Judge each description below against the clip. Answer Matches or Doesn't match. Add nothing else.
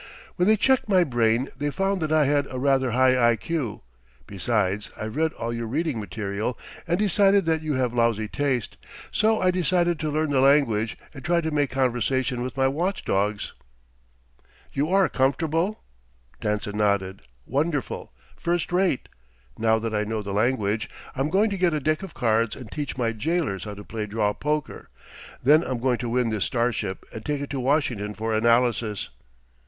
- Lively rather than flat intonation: Matches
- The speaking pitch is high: Doesn't match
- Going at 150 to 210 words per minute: Matches